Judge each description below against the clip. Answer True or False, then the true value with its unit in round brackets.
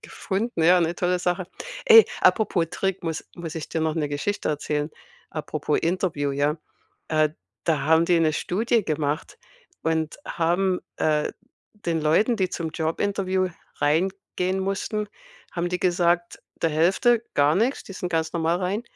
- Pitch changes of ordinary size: True (3.1 semitones)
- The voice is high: False (175 Hz)